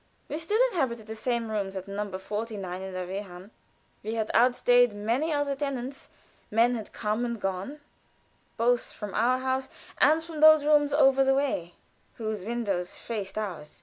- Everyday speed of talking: Yes, average, 165 wpm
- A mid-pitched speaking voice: No, high, 230 Hz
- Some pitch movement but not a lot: Yes, average, 4.9 semitones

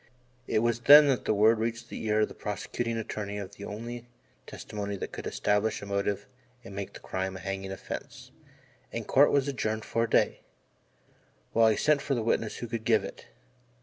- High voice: No, low, 110 Hz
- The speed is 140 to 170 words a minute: No, average, 195 wpm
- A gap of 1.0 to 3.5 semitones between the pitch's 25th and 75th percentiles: Yes, narrow, 2.5 semitones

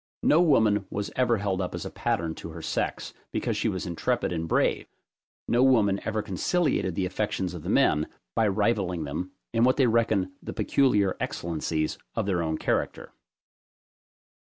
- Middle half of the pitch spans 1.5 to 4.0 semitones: No, average, 4.6 semitones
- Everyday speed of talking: Yes, average, 170 wpm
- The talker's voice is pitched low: Yes, low, 100 Hz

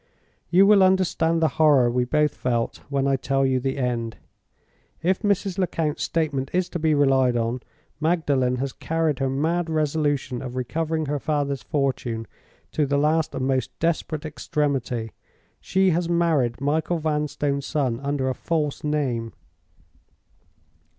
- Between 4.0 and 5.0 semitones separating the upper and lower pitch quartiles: No, average, 3.5 semitones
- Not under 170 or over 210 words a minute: No, average, 145 wpm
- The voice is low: No, medium, 145 Hz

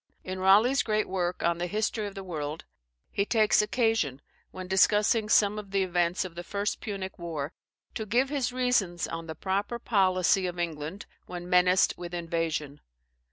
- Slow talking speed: No, average, 170 wpm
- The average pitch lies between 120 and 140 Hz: No, high, 190 Hz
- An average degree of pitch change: Yes, average, 3.5 semitones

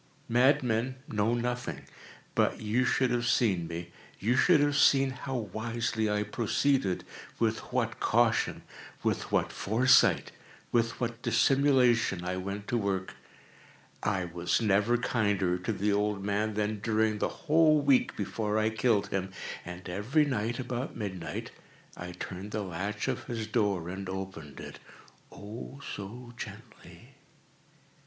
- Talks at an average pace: No, slow, 130 wpm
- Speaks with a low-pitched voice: Yes, low, 110 Hz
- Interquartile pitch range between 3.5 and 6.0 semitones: Yes, average, 3.8 semitones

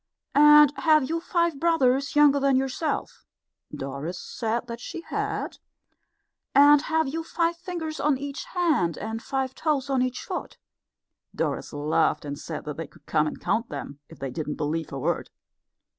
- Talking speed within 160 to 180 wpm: Yes, average, 165 wpm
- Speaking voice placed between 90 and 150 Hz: No, very high, 270 Hz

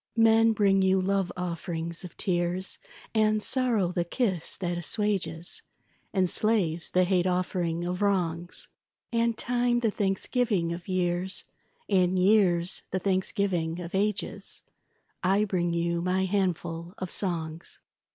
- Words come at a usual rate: No, slow, 130 wpm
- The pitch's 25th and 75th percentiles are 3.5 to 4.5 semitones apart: No, average, 2.7 semitones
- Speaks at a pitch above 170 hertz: Yes, medium, 185 Hz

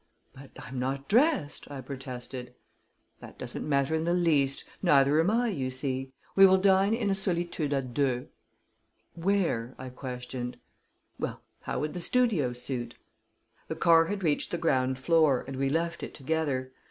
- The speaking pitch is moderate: Yes, medium, 145 Hz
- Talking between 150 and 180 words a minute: Yes, average, 165 wpm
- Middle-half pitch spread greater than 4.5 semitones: Yes, average, 4.9 semitones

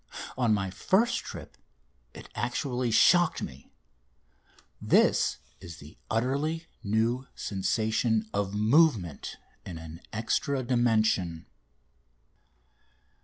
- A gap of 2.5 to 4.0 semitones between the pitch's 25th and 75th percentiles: No, average, 5.1 semitones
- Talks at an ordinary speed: No, slow, 90 wpm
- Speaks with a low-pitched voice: Yes, low, 110 Hz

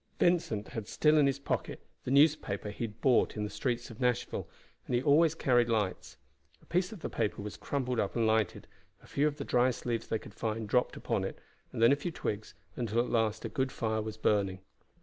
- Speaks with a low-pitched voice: Yes, low, 120 Hz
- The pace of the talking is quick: Yes, fast, 220 wpm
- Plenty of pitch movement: No, average, 4.3 semitones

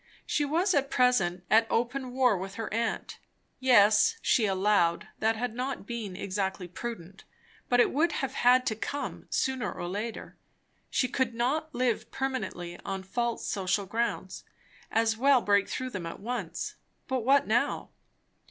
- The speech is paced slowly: No, average, 155 wpm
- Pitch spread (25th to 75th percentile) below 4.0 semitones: No, average, 4.4 semitones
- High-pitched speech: Yes, high, 230 Hz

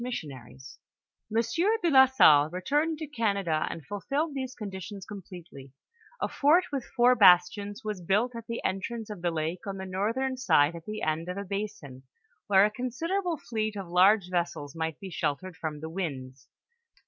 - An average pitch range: No, wide, 5.9 semitones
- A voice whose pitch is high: Yes, high, 200 Hz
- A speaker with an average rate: Yes, average, 170 wpm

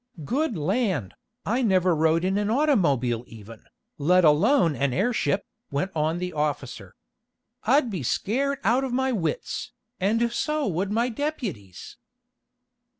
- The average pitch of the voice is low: No, high, 190 Hz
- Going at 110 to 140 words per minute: Yes, slow, 135 wpm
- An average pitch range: No, wide, 8.3 semitones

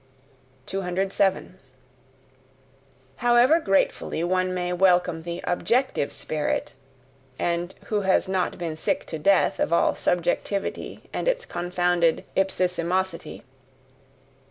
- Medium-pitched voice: Yes, medium, 180 Hz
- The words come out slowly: Yes, slow, 100 wpm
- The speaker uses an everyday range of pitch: No, narrow, 1.9 semitones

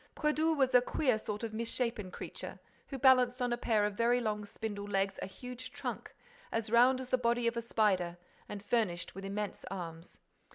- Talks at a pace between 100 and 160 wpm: No, average, 195 wpm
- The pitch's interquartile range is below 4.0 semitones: Yes, average, 3.4 semitones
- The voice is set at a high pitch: Yes, high, 230 Hz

